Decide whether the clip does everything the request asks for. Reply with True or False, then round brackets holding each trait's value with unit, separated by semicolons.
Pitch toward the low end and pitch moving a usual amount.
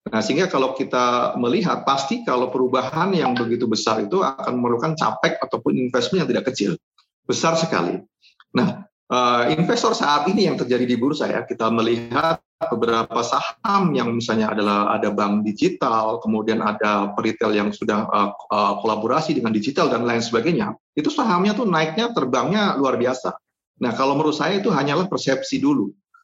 False (125 Hz; 7.8 semitones)